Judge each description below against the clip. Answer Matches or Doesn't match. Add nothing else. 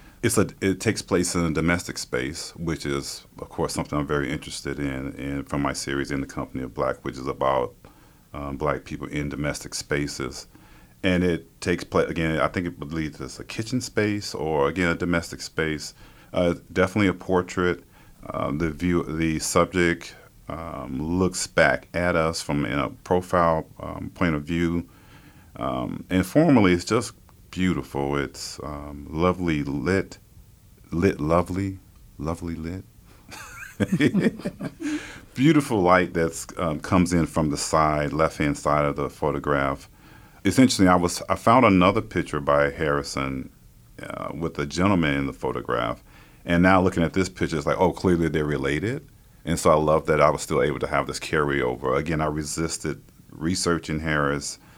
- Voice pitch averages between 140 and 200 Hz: Doesn't match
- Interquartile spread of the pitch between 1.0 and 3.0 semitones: Doesn't match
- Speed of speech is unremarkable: Matches